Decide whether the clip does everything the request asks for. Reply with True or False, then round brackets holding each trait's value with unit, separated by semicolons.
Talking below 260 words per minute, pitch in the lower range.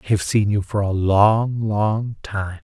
True (200 wpm; 105 Hz)